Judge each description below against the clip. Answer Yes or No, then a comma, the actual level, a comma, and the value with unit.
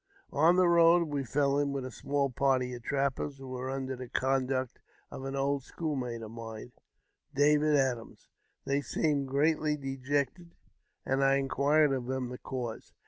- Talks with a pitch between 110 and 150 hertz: Yes, low, 135 Hz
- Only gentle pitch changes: Yes, narrow, 2.0 semitones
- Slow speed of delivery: No, average, 150 wpm